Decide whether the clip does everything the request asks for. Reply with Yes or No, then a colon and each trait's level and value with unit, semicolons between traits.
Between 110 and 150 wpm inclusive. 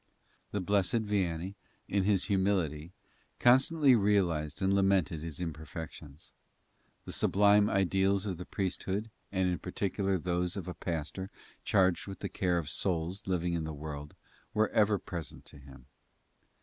Yes: average, 145 wpm